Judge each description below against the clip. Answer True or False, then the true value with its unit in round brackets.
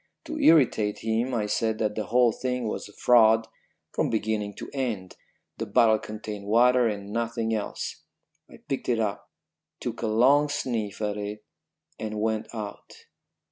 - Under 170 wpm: True (160 wpm)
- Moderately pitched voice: False (110 Hz)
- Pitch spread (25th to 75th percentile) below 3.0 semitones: True (2.4 semitones)